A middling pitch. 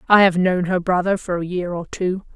Yes: medium, 180 Hz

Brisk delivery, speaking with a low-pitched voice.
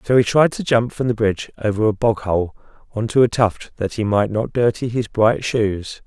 Yes: fast, 235 wpm; low, 110 Hz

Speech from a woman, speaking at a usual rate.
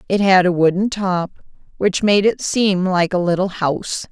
Yes: female; average, 190 wpm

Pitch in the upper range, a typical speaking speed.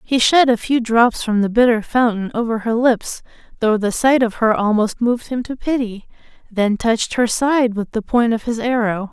No: high, 230 Hz; fast, 210 wpm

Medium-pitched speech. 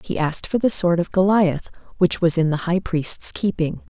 Yes: medium, 175 Hz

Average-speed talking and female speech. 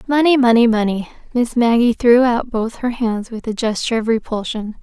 Yes: average, 185 wpm; female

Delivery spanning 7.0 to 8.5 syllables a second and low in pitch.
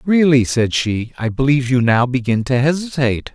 No: 5.4 syllables/s; low, 130 Hz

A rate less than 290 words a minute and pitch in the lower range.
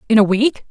No: fast, 255 wpm; high, 230 Hz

